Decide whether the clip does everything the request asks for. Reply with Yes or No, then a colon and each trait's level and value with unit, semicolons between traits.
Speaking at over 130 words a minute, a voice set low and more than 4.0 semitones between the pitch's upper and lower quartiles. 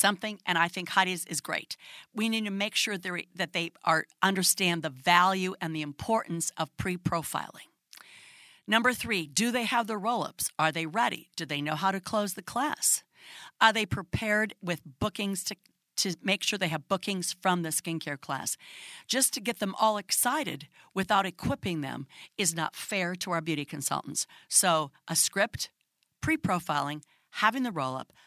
No: average, 180 wpm; medium, 185 Hz; average, 4.9 semitones